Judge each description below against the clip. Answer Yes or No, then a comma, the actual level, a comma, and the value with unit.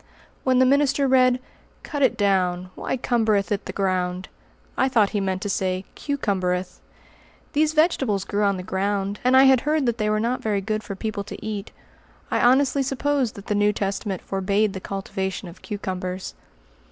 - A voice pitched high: Yes, high, 210 Hz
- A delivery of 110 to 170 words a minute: No, average, 185 wpm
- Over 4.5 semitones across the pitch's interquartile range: Yes, average, 4.9 semitones